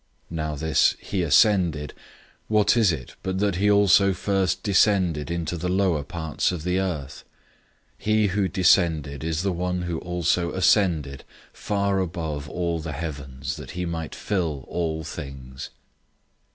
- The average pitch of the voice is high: No, very low, 85 Hz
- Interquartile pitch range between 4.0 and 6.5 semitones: No, average, 3.6 semitones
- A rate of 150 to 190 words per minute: Yes, average, 160 wpm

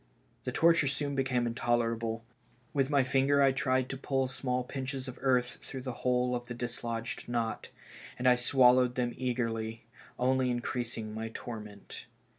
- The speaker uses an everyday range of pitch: No, narrow, 1.9 semitones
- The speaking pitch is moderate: No, low, 125 Hz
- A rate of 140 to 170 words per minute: Yes, average, 160 wpm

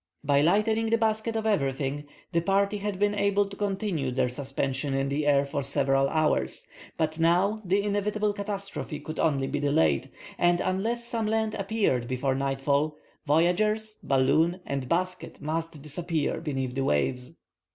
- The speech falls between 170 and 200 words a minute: No, average, 155 wpm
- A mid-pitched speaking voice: Yes, medium, 165 Hz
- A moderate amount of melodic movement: No, wide, 6.6 semitones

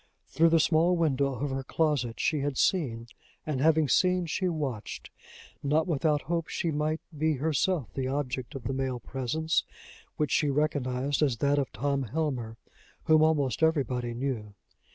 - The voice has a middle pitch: Yes, medium, 145 Hz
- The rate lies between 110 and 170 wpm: Yes, average, 160 wpm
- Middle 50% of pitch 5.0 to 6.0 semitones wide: No, average, 3.4 semitones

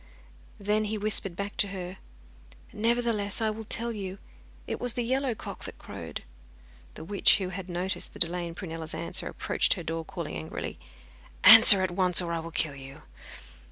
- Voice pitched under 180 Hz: No, high, 190 Hz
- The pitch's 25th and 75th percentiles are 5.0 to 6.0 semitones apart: No, average, 3.8 semitones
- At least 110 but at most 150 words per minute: No, average, 180 wpm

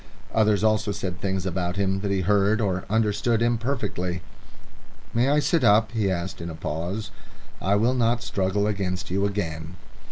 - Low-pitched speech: Yes, low, 100 Hz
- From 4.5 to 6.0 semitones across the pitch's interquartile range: No, average, 3.0 semitones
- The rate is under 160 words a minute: No, average, 165 wpm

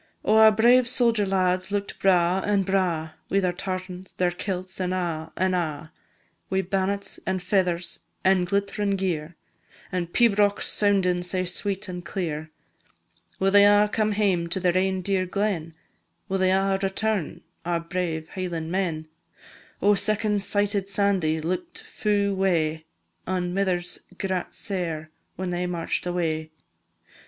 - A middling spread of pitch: No, narrow, 2.3 semitones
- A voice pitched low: No, medium, 185 Hz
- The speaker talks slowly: No, average, 145 wpm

